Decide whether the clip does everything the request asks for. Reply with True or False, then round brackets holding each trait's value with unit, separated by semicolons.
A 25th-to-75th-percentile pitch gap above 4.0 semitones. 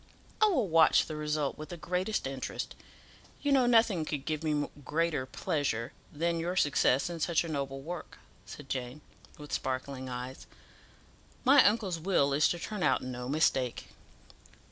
True (4.4 semitones)